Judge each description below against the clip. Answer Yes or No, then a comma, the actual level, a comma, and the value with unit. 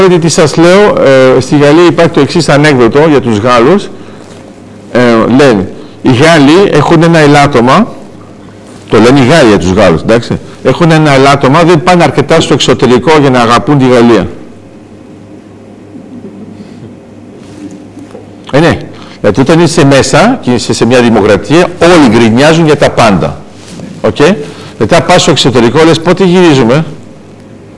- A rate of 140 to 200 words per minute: Yes, average, 145 wpm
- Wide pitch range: Yes, wide, 6.0 semitones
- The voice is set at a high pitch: No, low, 135 Hz